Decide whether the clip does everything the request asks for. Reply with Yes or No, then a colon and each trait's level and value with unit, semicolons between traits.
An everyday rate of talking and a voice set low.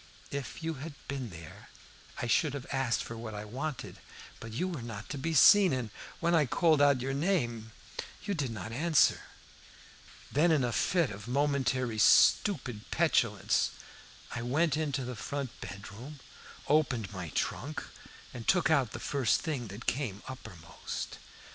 Yes: average, 160 wpm; low, 130 Hz